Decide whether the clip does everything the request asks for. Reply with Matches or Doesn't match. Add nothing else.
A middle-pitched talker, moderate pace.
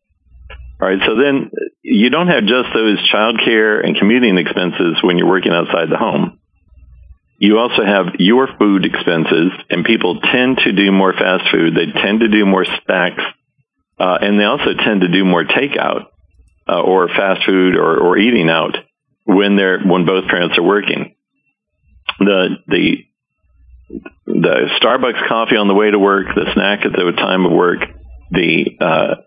Doesn't match